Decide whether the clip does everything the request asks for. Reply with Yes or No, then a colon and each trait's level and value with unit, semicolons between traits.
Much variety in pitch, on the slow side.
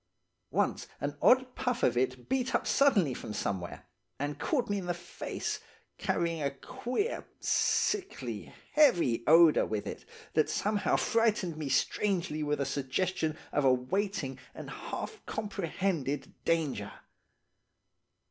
Yes: wide, 7.2 semitones; slow, 130 wpm